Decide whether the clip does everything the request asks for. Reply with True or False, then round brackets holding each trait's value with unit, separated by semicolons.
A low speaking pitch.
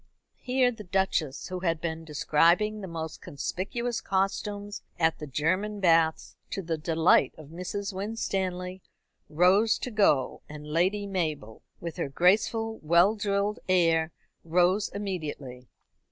False (180 Hz)